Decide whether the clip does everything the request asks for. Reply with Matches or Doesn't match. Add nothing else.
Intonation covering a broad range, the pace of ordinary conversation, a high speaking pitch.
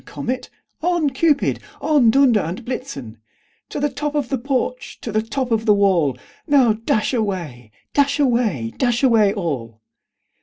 Matches